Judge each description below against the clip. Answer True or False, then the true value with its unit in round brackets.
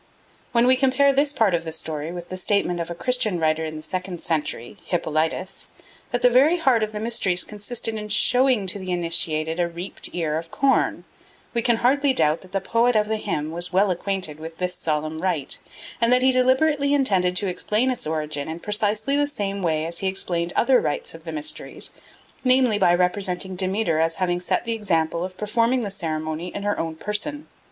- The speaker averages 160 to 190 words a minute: False (205 wpm)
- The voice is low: False (190 Hz)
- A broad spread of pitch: True (5.9 semitones)